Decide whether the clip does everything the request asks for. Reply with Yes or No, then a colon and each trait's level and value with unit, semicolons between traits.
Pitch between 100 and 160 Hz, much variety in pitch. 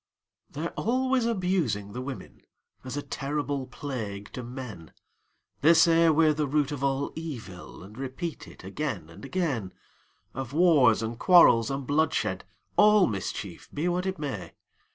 Yes: medium, 140 Hz; wide, 5.7 semitones